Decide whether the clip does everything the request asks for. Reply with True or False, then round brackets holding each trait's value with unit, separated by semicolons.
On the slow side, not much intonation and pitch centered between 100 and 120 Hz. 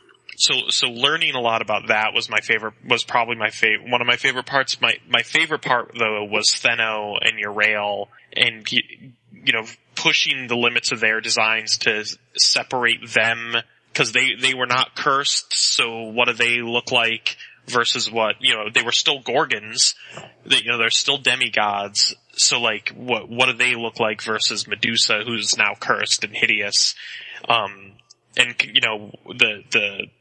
False (175 wpm; 2.2 semitones; 115 Hz)